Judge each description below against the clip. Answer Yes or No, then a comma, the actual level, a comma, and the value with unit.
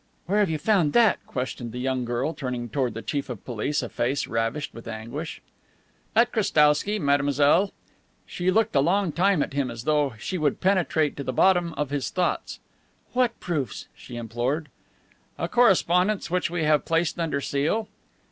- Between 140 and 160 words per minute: No, average, 175 wpm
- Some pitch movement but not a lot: No, wide, 5.8 semitones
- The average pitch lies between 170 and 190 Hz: No, medium, 150 Hz